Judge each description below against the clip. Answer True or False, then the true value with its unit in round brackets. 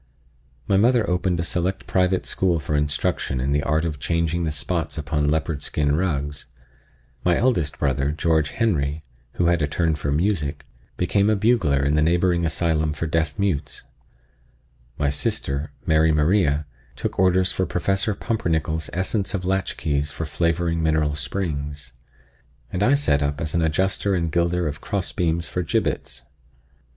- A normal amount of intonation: True (3.6 semitones)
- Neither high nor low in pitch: False (80 Hz)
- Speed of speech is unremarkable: True (155 wpm)